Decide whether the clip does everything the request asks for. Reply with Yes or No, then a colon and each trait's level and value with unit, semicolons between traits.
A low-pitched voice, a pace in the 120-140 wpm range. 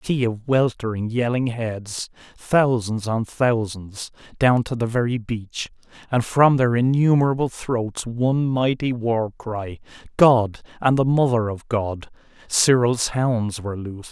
Yes: low, 120 Hz; slow, 135 wpm